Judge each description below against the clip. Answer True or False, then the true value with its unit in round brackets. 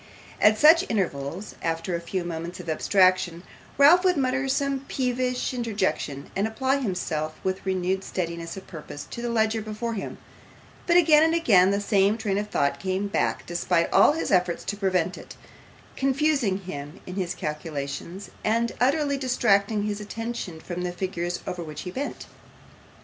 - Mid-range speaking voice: False (200 Hz)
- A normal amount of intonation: False (5.8 semitones)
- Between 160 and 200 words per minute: True (165 wpm)